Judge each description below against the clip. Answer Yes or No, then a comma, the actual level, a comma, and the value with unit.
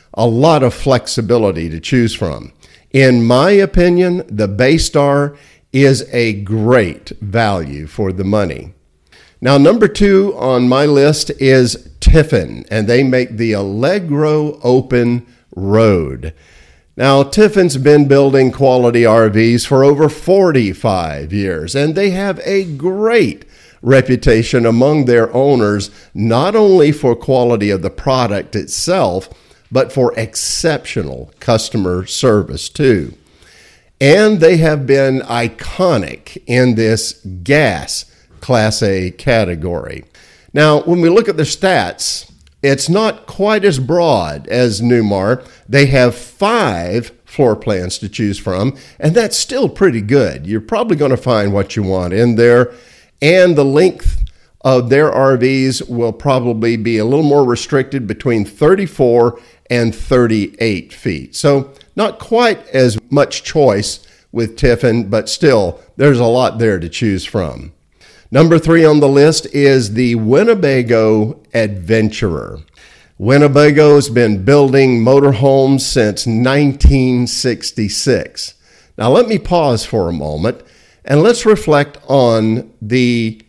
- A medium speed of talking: No, slow, 130 wpm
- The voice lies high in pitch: No, low, 125 Hz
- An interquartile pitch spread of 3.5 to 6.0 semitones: Yes, average, 4.6 semitones